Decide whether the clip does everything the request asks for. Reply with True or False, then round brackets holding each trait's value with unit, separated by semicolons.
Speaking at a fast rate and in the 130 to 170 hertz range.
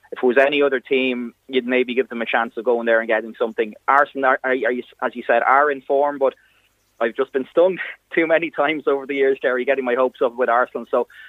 True (250 wpm; 135 Hz)